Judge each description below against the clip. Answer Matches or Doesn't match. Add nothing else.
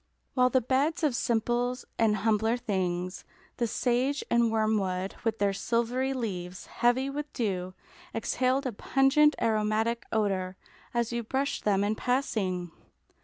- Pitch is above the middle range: Matches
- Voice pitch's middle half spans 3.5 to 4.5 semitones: Matches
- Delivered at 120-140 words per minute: Matches